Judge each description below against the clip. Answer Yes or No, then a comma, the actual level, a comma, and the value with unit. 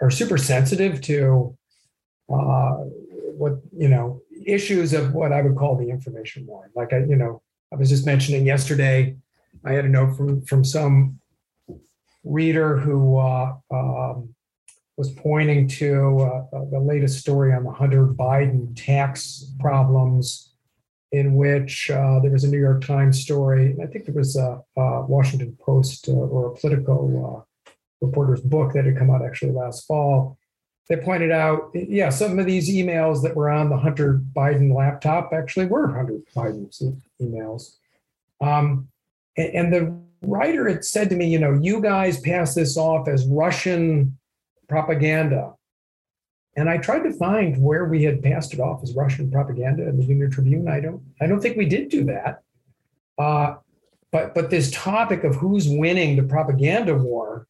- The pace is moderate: Yes, average, 165 wpm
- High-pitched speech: No, medium, 140 Hz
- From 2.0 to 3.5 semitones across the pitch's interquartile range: Yes, average, 2.8 semitones